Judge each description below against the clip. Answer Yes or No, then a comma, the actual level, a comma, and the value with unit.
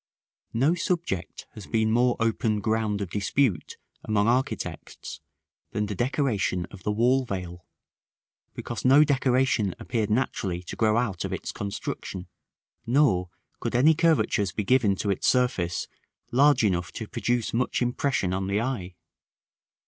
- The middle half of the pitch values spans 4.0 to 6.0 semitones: Yes, average, 4.6 semitones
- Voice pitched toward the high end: No, low, 110 Hz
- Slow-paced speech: No, average, 150 wpm